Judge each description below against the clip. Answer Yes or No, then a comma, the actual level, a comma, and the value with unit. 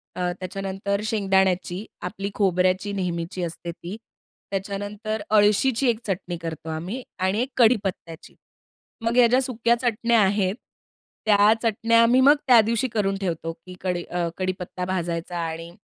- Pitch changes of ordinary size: Yes, average, 3.6 semitones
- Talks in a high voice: Yes, high, 195 Hz